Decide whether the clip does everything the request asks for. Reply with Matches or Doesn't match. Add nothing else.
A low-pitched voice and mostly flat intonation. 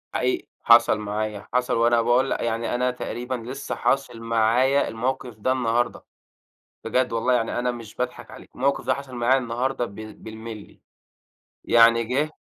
Matches